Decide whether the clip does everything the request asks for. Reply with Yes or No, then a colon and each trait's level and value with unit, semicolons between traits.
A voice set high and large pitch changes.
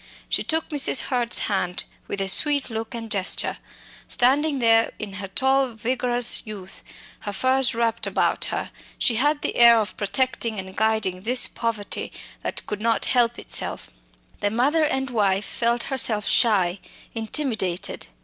No: high, 230 Hz; average, 4.0 semitones